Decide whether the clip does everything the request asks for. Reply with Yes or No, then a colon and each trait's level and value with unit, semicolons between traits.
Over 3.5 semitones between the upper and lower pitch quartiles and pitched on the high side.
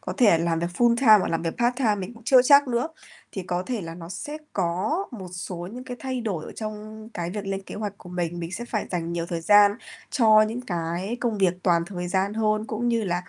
Yes: average, 4.9 semitones; high, 205 Hz